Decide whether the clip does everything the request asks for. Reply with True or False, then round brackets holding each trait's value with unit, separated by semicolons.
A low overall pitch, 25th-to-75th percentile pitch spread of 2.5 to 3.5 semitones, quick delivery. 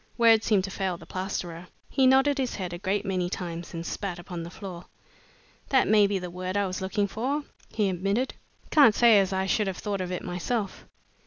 False (195 Hz; 3.1 semitones; 215 wpm)